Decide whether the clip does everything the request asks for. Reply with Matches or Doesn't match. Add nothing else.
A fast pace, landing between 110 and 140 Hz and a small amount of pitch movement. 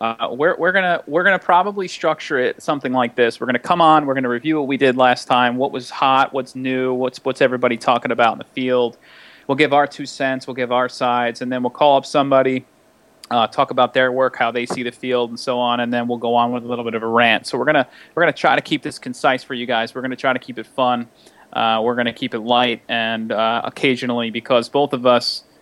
Matches